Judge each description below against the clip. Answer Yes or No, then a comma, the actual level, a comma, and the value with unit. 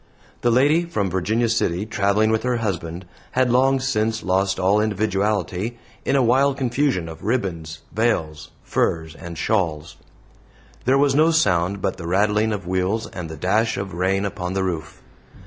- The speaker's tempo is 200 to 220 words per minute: No, average, 165 wpm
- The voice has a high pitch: No, low, 100 Hz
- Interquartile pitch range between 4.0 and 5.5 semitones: Yes, average, 4.6 semitones